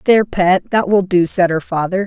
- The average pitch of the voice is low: No, medium, 185 Hz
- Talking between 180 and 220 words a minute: No, fast, 230 wpm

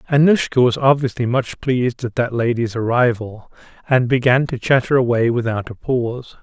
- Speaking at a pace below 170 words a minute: Yes, average, 160 wpm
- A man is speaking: Yes, male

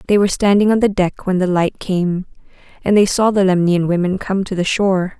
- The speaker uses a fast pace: Yes, fast, 230 wpm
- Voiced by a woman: Yes, female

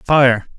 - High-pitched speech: No, low, 130 Hz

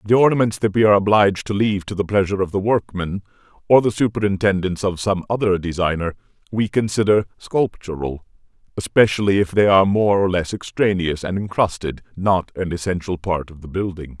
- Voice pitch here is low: Yes, very low, 95 Hz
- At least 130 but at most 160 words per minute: No, average, 170 wpm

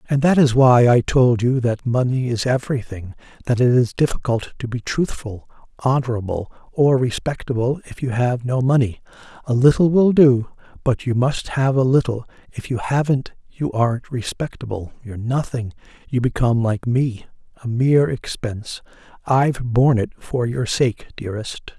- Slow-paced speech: No, average, 160 wpm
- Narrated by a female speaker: No, male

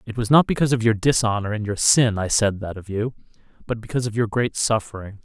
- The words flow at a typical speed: No, fast, 240 wpm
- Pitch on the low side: Yes, low, 110 Hz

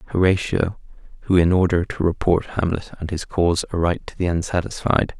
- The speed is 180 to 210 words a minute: No, average, 160 wpm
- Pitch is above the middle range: No, very low, 85 Hz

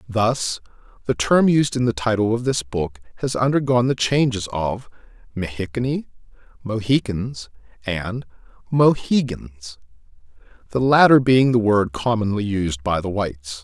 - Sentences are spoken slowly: Yes, slow, 130 wpm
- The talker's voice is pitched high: No, low, 115 Hz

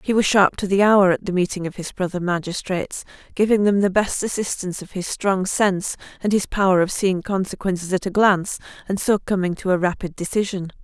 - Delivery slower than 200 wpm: No, fast, 205 wpm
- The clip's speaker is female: Yes, female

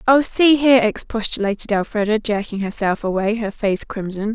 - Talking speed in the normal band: Yes, average, 150 wpm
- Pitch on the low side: No, high, 220 Hz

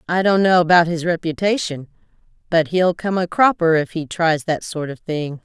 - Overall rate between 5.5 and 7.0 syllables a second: No, 4.9 syllables/s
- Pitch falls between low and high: Yes, medium, 170 Hz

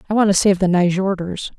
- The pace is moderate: No, fast, 225 wpm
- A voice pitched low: No, high, 190 Hz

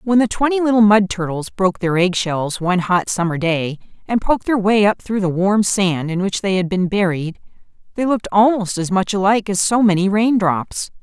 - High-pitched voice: Yes, high, 195 Hz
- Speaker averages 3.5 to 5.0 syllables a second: No, 5.3 syllables/s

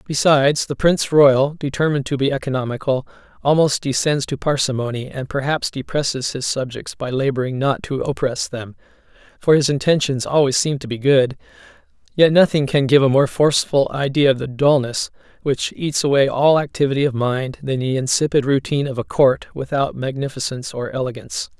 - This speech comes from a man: Yes, male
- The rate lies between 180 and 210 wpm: No, average, 165 wpm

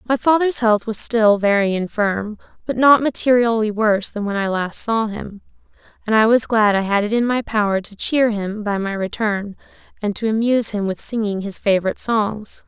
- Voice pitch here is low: No, high, 215 Hz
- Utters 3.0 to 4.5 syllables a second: No, 5.1 syllables/s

